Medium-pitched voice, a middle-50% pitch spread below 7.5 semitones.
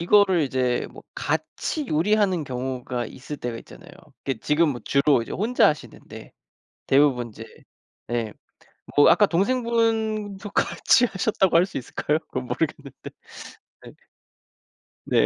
No: medium, 155 Hz; wide, 8.0 semitones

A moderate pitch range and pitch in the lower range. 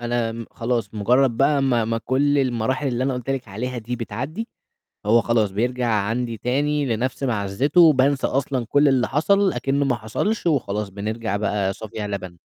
Yes: average, 3.7 semitones; low, 120 Hz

